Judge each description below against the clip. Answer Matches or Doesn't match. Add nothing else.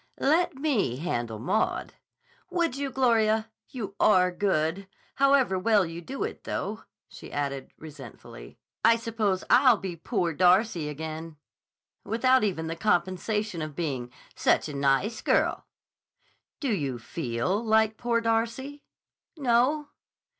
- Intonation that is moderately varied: Doesn't match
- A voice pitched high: Matches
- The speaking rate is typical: Doesn't match